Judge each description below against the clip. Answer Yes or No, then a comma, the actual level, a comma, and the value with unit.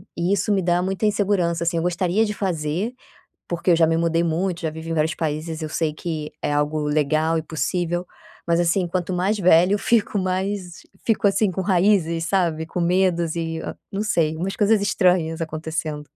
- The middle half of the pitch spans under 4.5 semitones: Yes, average, 2.8 semitones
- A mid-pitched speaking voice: Yes, medium, 170 Hz